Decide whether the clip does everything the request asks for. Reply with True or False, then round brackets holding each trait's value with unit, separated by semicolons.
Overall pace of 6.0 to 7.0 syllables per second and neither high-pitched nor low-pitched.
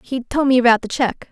False (6.7 syllables/s; 245 Hz)